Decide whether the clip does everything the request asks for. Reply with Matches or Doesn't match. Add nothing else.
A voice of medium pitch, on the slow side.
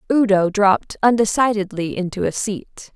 Doesn't match